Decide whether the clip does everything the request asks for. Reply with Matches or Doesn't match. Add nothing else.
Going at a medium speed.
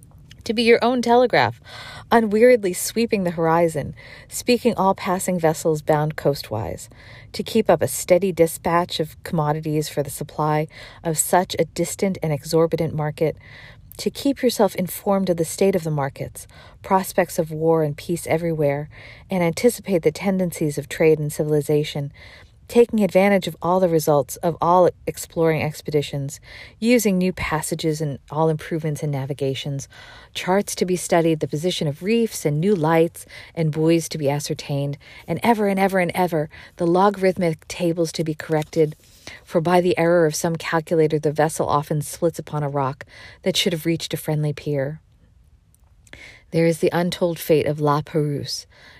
Matches